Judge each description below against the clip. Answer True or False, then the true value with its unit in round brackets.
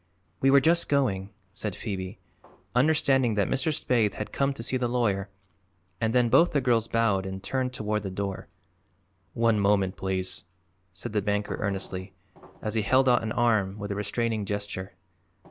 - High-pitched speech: False (105 Hz)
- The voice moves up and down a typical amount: True (4.0 semitones)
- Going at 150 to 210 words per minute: True (170 wpm)